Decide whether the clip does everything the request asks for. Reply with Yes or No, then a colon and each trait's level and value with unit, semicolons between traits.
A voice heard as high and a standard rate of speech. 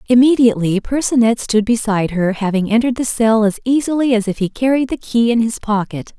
Yes: high, 225 Hz; average, 195 wpm